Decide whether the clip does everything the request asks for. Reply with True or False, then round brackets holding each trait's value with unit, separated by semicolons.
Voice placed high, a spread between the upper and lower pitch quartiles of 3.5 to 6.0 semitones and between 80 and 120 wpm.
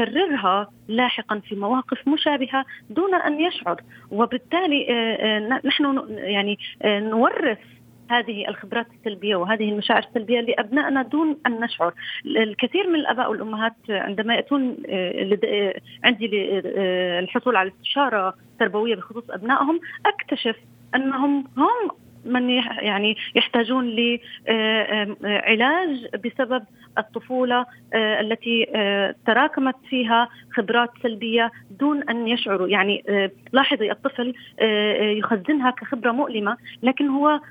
True (235 Hz; 4.0 semitones; 95 wpm)